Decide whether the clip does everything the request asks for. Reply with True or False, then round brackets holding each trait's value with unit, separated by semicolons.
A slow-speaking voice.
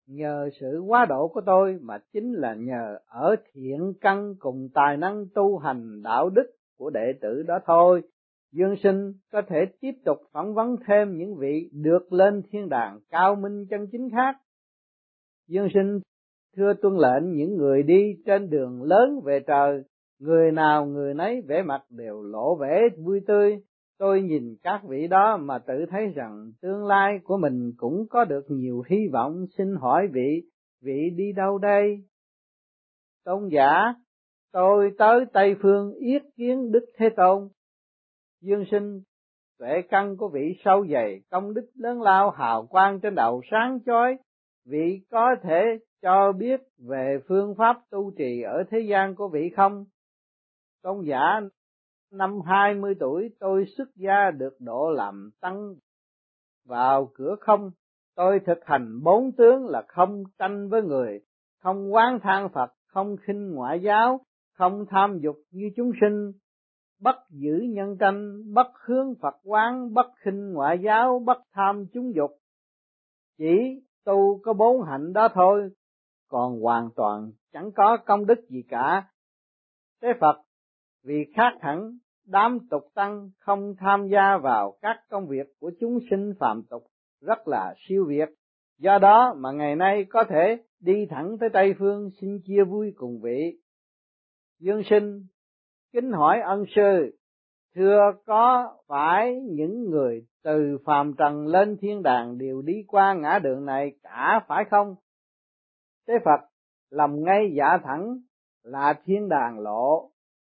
True (155 wpm)